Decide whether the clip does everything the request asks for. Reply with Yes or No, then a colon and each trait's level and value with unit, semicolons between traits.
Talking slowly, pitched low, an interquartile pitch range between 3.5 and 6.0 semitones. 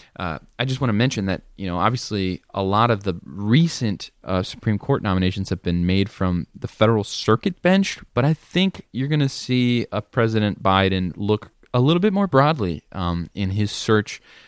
No: average, 195 wpm; low, 110 Hz; average, 4.9 semitones